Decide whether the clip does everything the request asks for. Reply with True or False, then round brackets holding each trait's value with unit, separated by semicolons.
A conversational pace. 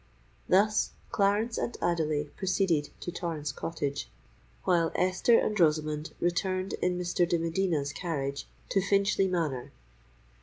False (120 wpm)